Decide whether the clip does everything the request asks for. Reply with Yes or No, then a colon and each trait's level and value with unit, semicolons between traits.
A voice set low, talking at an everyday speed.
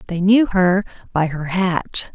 No: medium, 185 Hz; average, 170 wpm